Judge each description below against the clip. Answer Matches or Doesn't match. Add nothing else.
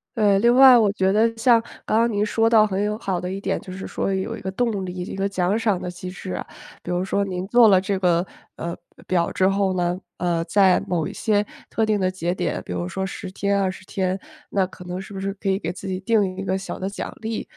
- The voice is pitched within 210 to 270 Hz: Doesn't match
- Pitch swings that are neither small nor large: Doesn't match